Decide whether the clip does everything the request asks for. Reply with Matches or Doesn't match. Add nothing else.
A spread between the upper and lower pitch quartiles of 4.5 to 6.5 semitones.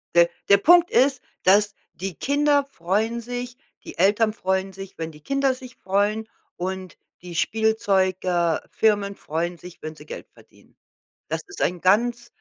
Matches